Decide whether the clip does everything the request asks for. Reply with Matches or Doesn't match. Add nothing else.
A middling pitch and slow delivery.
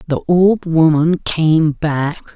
Matches